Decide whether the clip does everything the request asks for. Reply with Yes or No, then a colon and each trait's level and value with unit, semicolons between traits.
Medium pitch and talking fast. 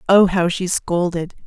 No: medium, 180 Hz; average, 165 wpm